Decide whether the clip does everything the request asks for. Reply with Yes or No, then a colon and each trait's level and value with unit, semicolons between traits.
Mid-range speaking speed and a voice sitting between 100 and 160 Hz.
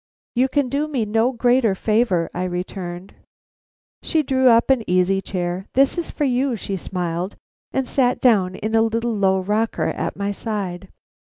No: average, 170 wpm; high, 220 Hz